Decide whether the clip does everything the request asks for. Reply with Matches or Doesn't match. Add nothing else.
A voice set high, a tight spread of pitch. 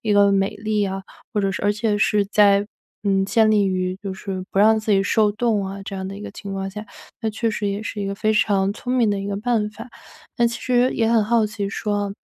Matches